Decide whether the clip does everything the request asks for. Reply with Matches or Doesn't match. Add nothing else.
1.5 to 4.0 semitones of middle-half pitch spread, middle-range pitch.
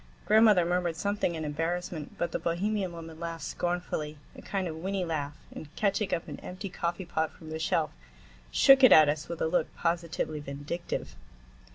Matches